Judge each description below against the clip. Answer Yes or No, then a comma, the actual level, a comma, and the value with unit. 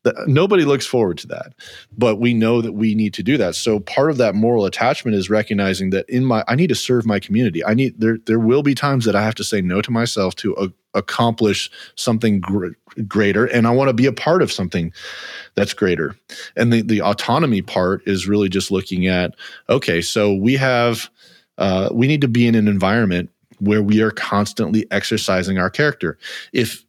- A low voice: Yes, low, 110 Hz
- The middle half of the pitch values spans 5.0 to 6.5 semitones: No, average, 3.3 semitones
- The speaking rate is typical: No, fast, 210 wpm